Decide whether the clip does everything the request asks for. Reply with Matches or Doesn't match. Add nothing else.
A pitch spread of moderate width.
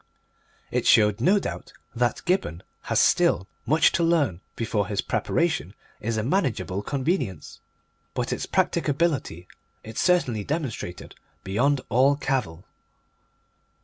Doesn't match